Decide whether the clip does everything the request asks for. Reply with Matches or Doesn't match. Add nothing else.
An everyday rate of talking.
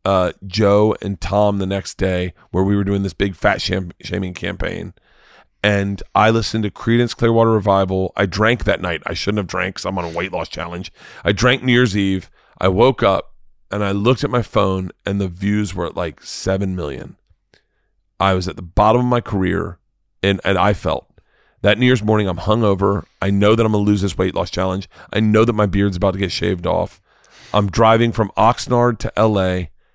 Doesn't match